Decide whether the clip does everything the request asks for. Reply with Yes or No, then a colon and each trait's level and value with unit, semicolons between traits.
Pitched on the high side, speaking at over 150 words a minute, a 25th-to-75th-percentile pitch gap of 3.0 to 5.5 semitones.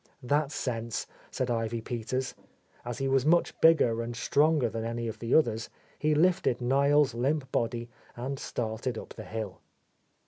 No: low, 125 Hz; average, 160 wpm; average, 3.4 semitones